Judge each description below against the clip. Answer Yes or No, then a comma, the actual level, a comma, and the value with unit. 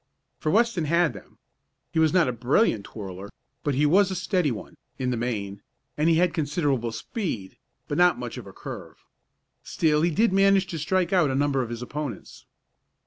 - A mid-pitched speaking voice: Yes, medium, 150 Hz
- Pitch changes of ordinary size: No, wide, 6.5 semitones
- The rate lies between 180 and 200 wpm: Yes, average, 195 wpm